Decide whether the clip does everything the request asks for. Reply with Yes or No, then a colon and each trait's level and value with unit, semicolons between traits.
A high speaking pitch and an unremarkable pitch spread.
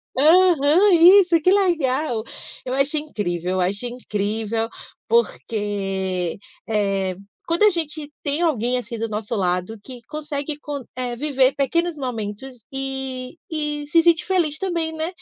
No: very high, 270 Hz; wide, 6.4 semitones